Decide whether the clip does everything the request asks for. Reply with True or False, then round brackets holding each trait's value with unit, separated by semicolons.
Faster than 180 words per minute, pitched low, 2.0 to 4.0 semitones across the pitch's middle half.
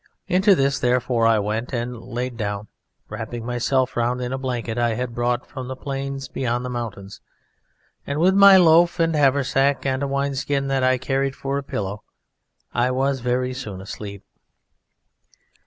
False (170 wpm; 130 Hz; 2.6 semitones)